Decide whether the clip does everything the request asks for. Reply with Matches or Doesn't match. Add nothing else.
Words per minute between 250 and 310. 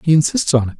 Matches